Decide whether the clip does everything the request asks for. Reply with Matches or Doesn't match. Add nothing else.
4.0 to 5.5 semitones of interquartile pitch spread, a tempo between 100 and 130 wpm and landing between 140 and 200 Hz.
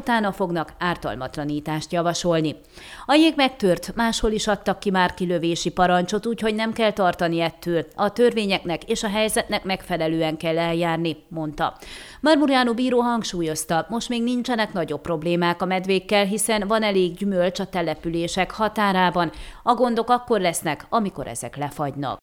Doesn't match